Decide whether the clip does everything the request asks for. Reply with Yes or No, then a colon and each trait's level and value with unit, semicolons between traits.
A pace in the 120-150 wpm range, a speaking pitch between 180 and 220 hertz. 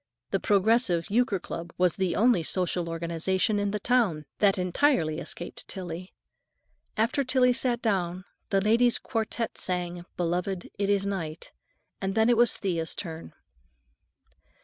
Yes: average, 140 wpm; high, 190 Hz